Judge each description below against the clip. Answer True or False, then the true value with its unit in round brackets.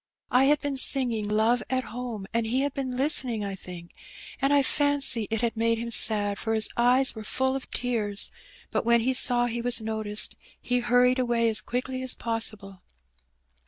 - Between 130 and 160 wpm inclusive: False (190 wpm)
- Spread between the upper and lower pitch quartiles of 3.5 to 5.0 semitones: False (2.8 semitones)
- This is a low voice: False (235 Hz)